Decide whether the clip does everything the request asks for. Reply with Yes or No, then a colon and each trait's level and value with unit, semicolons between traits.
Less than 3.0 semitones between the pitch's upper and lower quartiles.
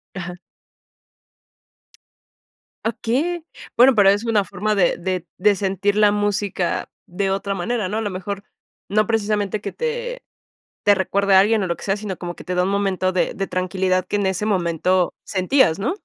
Yes: narrow, 2.4 semitones